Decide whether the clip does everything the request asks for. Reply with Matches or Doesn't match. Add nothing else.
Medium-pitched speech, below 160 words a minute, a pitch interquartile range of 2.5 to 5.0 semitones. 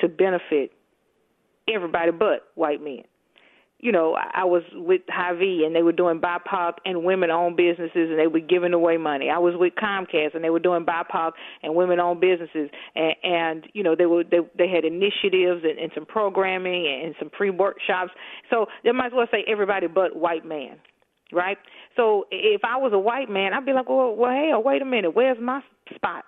Doesn't match